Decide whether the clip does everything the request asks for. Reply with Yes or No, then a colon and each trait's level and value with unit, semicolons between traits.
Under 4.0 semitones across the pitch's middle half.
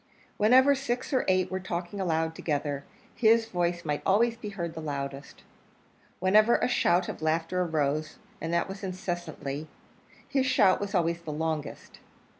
No: average, 4.3 semitones